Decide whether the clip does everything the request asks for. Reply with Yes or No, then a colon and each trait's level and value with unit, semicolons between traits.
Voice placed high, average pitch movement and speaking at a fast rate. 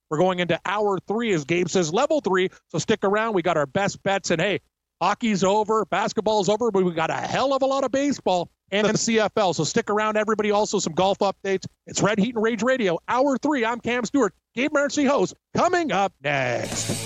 Yes: high, 205 Hz; average, 3.7 semitones; fast, 220 wpm